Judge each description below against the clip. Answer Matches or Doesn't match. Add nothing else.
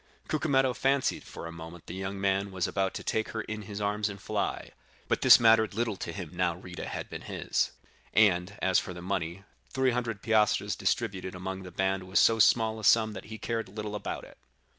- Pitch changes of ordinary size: Matches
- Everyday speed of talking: Doesn't match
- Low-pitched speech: Matches